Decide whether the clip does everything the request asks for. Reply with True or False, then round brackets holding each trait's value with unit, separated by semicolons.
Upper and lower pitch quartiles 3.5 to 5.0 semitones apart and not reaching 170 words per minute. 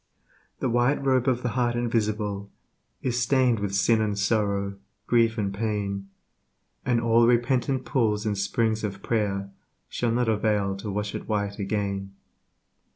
False (2.9 semitones; 150 wpm)